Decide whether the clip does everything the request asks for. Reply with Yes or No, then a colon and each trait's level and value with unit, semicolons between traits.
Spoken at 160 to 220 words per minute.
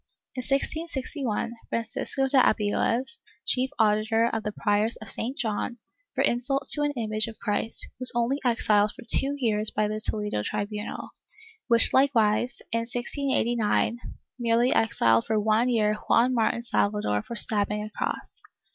No: average, 145 wpm